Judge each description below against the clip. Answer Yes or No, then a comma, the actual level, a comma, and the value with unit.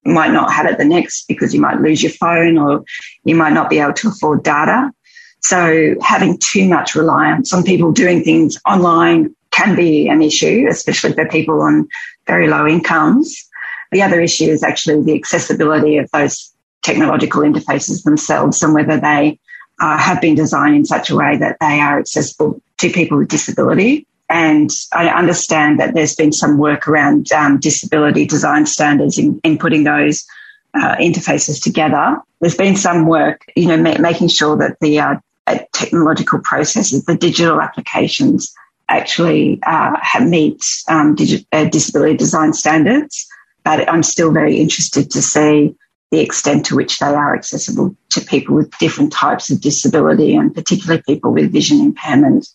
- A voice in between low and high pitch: Yes, medium, 160 Hz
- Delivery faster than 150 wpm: Yes, average, 170 wpm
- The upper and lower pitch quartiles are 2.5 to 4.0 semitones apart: Yes, average, 3.4 semitones